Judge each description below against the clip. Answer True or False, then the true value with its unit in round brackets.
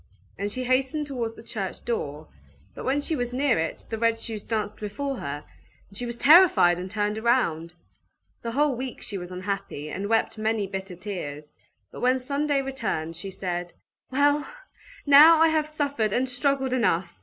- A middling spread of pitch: False (5.9 semitones)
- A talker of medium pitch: False (230 Hz)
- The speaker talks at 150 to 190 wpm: True (180 wpm)